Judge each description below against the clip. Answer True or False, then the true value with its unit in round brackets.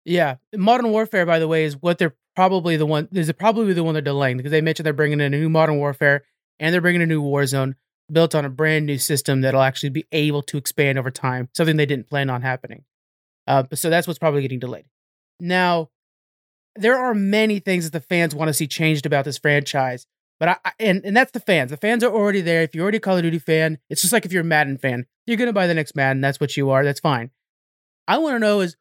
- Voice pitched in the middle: True (155 Hz)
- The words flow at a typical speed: False (255 wpm)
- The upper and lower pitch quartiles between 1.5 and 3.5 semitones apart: False (4.1 semitones)